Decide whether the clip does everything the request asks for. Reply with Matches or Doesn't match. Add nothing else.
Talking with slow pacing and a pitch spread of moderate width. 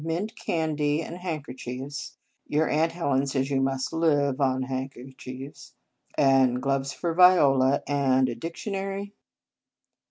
Matches